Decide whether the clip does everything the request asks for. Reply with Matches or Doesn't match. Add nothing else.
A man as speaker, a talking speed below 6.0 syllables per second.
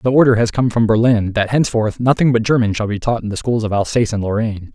Doesn't match